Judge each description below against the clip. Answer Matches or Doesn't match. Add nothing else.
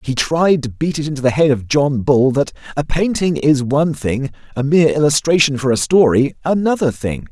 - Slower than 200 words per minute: Doesn't match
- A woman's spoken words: Doesn't match